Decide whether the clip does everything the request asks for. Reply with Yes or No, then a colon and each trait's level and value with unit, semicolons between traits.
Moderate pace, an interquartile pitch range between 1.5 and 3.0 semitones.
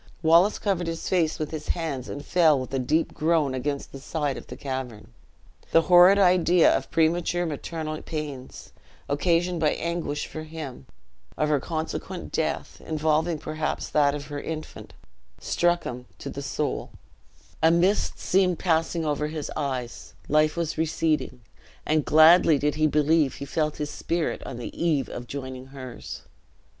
Yes: average, 160 wpm; narrow, 2.6 semitones